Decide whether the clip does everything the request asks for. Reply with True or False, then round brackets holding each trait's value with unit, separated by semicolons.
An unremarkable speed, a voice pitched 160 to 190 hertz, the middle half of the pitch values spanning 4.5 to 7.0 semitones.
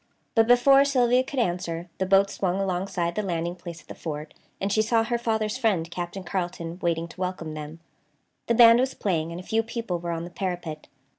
False (210 wpm; 185 Hz; 4.9 semitones)